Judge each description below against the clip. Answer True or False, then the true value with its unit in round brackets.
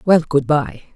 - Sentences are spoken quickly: False (190 wpm)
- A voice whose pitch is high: False (150 Hz)